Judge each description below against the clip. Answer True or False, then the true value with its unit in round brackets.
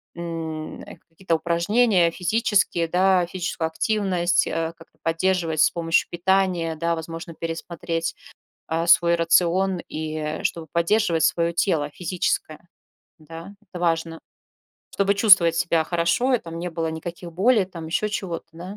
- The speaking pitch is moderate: True (170 Hz)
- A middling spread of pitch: False (2.2 semitones)